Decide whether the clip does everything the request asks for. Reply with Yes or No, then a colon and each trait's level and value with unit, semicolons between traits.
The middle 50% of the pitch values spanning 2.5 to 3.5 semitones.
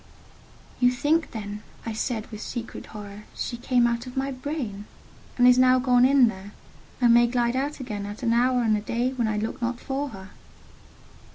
Yes: average, 2.9 semitones